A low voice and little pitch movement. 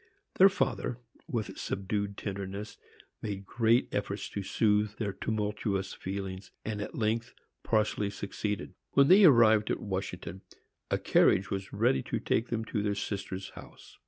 Yes: low, 105 Hz; narrow, 2.1 semitones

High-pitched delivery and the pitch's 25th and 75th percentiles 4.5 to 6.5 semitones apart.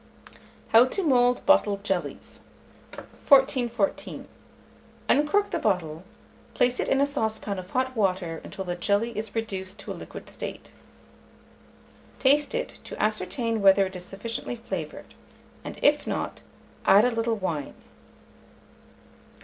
Yes: high, 225 Hz; average, 5.1 semitones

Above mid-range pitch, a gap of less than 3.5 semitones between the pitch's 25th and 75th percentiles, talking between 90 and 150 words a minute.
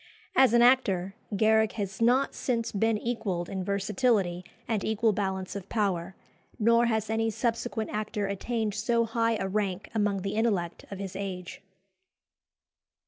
Yes: high, 210 Hz; average, 2.9 semitones; average, 145 wpm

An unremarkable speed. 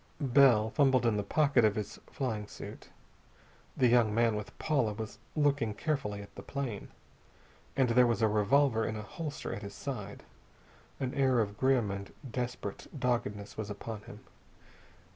Yes: average, 160 wpm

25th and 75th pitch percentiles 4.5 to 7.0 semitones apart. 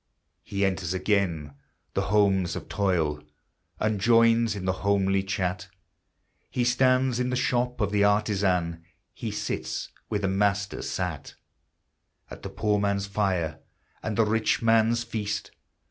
No: average, 3.1 semitones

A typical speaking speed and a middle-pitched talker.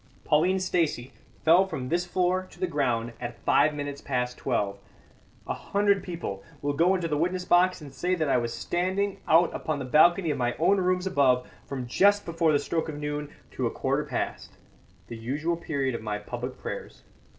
Yes: average, 195 wpm; medium, 155 Hz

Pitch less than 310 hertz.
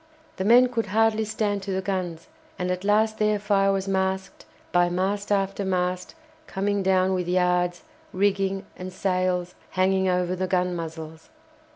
Yes: high, 190 Hz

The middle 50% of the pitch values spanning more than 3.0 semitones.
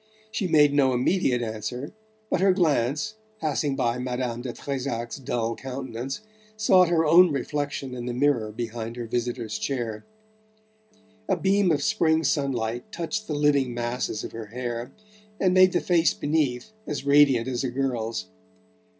Yes: average, 4.5 semitones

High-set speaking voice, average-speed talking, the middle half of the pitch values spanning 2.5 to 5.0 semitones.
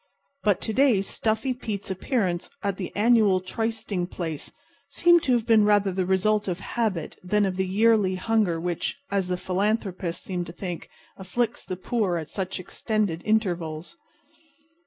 Yes: high, 195 Hz; average, 155 wpm; average, 3.4 semitones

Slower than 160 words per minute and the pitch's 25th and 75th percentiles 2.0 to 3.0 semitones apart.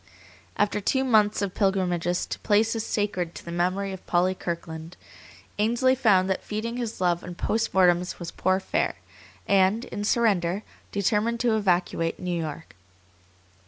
No: average, 150 wpm; average, 3.5 semitones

